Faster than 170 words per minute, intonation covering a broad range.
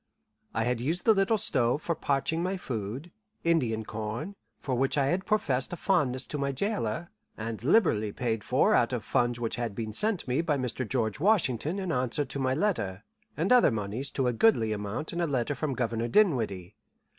Yes: average, 195 wpm; wide, 6.6 semitones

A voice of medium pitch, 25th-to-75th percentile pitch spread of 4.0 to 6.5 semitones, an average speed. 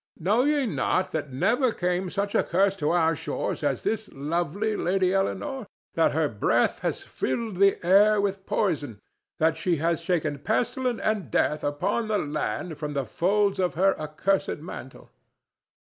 Yes: medium, 180 Hz; average, 4.9 semitones; average, 160 wpm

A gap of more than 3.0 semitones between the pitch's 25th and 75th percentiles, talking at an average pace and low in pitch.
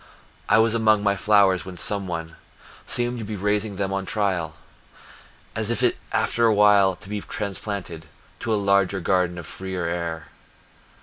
No: narrow, 2.6 semitones; average, 160 wpm; low, 100 Hz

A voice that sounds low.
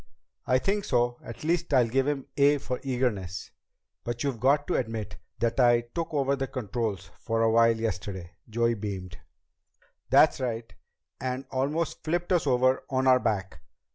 Yes: low, 125 Hz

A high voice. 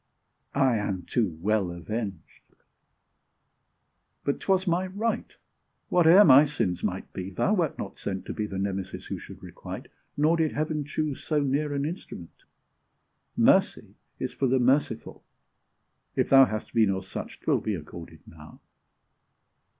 No: low, 125 Hz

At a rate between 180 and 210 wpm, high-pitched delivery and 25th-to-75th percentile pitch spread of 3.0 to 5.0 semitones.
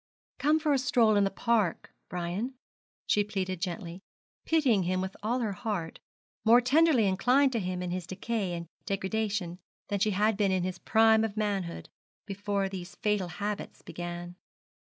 No: average, 165 wpm; high, 200 Hz; average, 3.4 semitones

